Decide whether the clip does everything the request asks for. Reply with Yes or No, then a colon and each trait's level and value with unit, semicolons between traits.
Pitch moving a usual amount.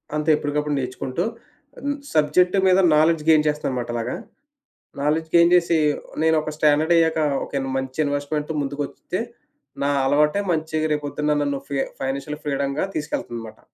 No: narrow, 2.0 semitones